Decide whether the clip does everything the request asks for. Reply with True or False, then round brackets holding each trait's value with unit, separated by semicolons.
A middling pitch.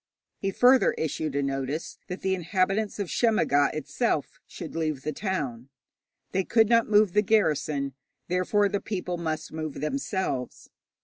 True (180 Hz)